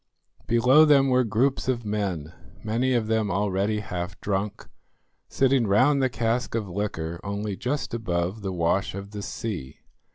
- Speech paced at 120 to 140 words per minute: No, average, 155 wpm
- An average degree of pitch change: Yes, average, 4.1 semitones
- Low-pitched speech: Yes, low, 105 Hz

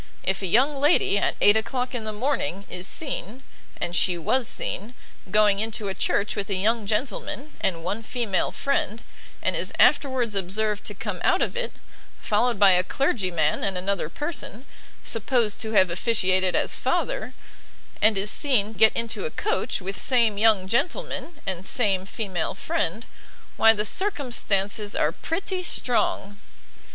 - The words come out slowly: No, average, 160 wpm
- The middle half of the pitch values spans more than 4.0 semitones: Yes, average, 4.4 semitones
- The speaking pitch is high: Yes, high, 215 Hz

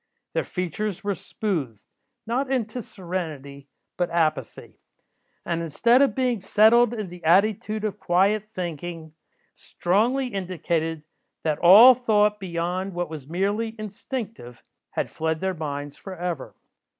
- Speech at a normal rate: No, slow, 125 wpm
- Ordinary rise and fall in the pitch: Yes, average, 4.6 semitones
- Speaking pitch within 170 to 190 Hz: Yes, medium, 185 Hz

